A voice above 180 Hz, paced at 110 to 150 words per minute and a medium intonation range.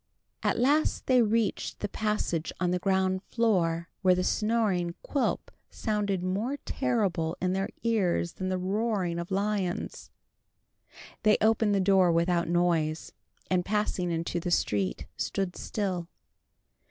Yes: high, 190 Hz; average, 140 wpm; average, 3.4 semitones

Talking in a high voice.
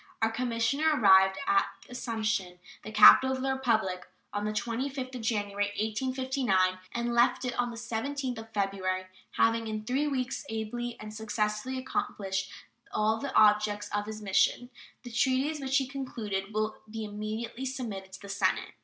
Yes: high, 225 Hz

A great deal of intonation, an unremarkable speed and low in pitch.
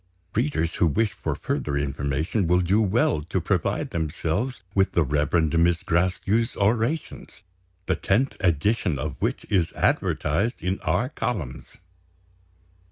No: wide, 5.8 semitones; slow, 130 wpm; very low, 90 Hz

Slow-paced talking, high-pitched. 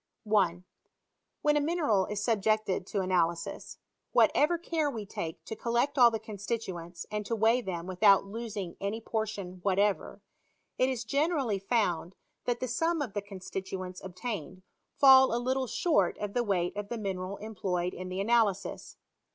No: average, 165 wpm; high, 210 Hz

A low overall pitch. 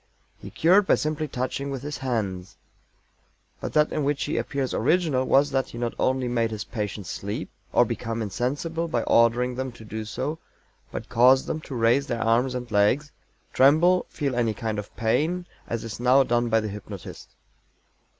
Yes: low, 125 Hz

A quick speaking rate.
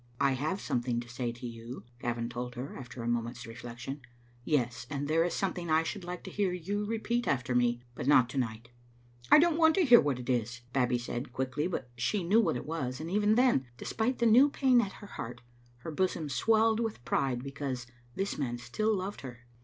Yes: fast, 225 wpm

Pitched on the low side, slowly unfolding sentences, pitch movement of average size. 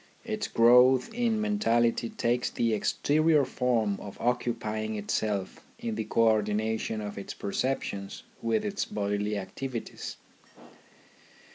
Yes: low, 115 Hz; slow, 115 wpm; average, 3.9 semitones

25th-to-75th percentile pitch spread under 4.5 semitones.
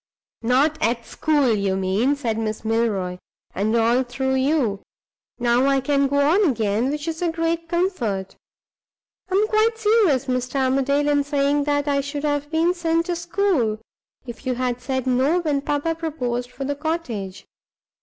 No: average, 4.9 semitones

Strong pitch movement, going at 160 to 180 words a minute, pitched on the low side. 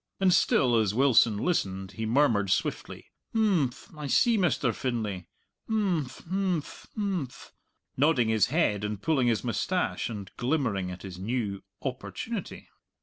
No: wide, 7.6 semitones; slow, 135 wpm; low, 125 Hz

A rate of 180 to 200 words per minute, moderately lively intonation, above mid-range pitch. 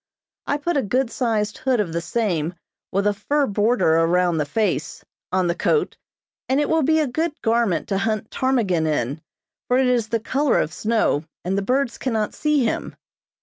No: average, 190 wpm; wide, 6.4 semitones; high, 220 Hz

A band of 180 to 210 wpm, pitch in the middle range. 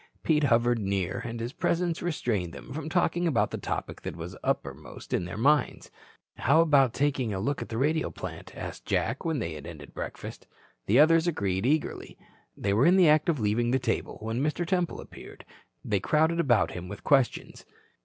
No: average, 195 wpm; low, 130 Hz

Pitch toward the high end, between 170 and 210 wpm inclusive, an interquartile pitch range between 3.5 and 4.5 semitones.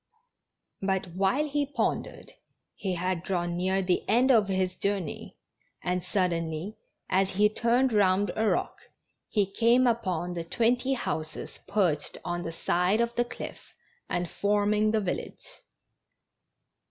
No: high, 195 Hz; slow, 135 wpm; average, 3.9 semitones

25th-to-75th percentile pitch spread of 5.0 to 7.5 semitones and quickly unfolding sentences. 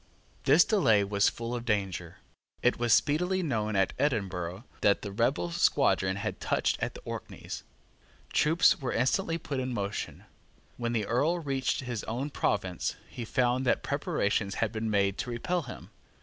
No: wide, 5.4 semitones; average, 165 wpm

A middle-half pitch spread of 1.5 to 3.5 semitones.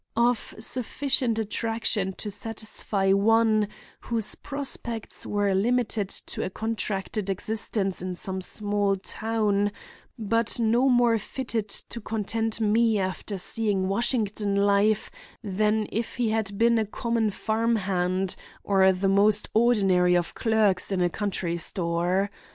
Yes: average, 2.7 semitones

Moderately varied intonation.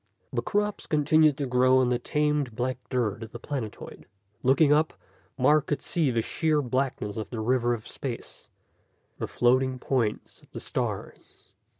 Yes: average, 3.6 semitones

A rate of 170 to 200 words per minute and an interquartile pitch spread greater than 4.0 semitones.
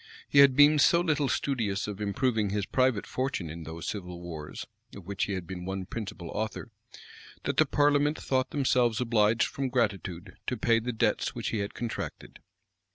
Yes: average, 180 wpm; average, 5.2 semitones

